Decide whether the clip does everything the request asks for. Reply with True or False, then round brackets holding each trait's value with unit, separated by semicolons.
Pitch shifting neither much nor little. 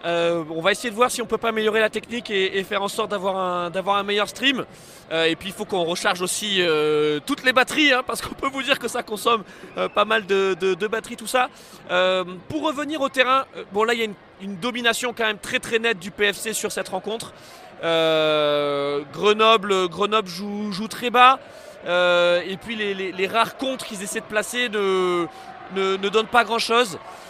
True (3.8 semitones)